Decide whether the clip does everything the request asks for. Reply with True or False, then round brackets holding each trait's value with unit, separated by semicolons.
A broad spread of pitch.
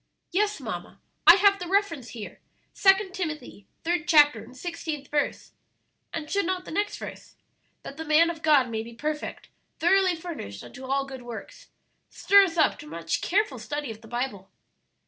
True (6.0 semitones)